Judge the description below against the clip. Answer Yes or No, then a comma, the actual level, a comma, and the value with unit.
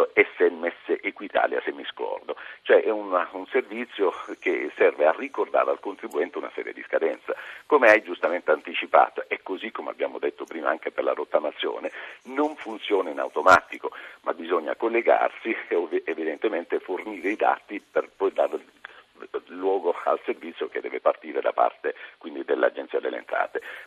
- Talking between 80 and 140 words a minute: No, average, 155 wpm